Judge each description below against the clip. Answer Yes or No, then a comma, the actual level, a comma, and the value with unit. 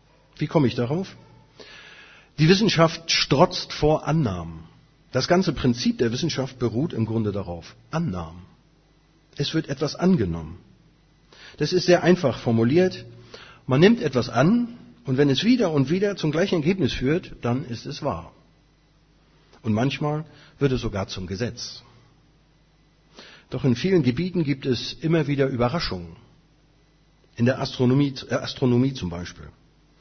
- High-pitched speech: No, medium, 140 Hz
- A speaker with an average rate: Yes, average, 140 wpm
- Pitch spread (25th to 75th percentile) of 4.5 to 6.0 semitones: Yes, average, 5.0 semitones